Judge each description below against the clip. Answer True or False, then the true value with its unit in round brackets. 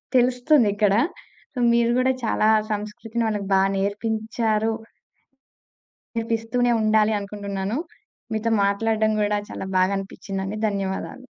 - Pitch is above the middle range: True (215 Hz)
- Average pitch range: False (2.2 semitones)